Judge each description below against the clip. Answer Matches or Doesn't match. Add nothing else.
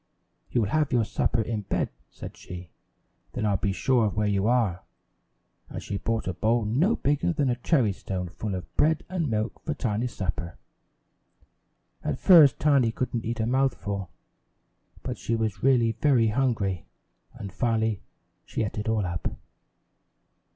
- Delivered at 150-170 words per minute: Matches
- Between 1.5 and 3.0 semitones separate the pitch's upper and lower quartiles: Doesn't match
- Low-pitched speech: Matches